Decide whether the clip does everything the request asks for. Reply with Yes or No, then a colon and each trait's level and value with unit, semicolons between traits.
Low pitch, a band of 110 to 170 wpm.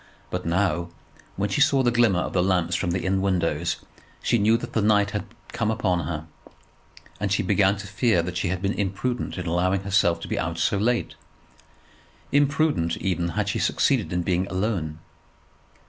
No: very low, 95 Hz; average, 185 wpm